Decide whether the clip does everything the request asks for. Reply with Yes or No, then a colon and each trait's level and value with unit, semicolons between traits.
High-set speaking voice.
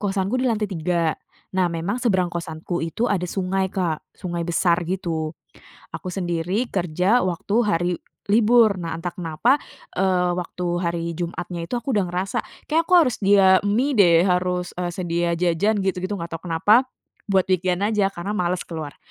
No: medium, 180 Hz